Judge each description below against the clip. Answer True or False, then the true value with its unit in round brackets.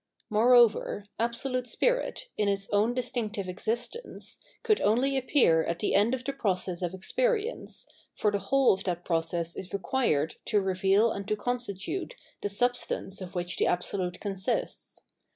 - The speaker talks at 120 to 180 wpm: True (150 wpm)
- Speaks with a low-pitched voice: False (210 Hz)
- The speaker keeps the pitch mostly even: False (4.8 semitones)